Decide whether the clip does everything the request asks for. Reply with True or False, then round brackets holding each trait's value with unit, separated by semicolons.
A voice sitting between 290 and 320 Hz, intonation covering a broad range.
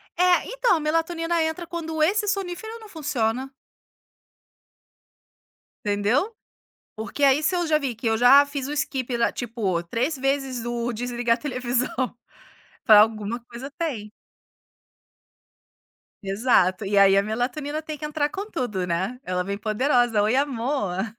False (255 Hz; 5.7 semitones)